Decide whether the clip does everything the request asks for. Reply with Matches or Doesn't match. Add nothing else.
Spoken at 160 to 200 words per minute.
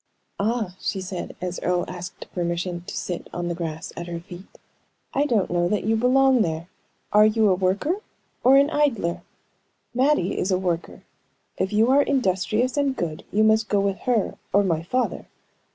Matches